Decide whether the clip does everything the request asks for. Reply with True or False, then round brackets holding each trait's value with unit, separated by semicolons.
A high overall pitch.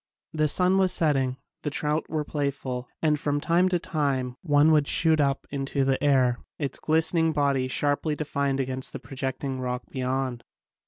False (145 Hz)